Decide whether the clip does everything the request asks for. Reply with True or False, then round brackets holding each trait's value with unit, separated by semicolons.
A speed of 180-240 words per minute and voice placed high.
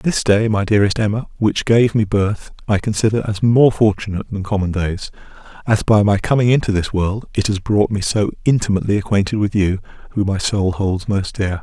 False (200 wpm; 105 Hz)